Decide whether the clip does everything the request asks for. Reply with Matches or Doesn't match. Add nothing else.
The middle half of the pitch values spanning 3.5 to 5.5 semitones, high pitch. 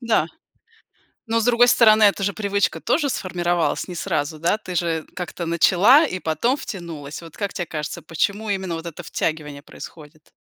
Doesn't match